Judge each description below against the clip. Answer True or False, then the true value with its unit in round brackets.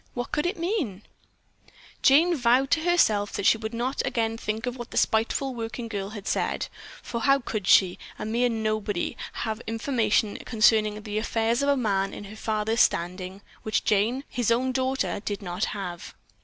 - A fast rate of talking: False (180 wpm)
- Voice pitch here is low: False (225 Hz)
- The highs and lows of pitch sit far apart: False (3.3 semitones)